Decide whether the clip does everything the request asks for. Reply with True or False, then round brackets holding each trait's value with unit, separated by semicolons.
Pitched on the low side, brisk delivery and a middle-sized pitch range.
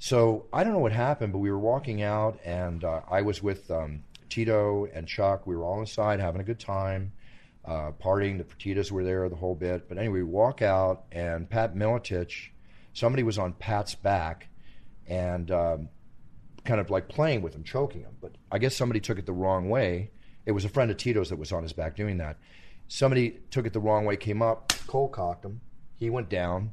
True (100 Hz; 215 wpm; 3.8 semitones)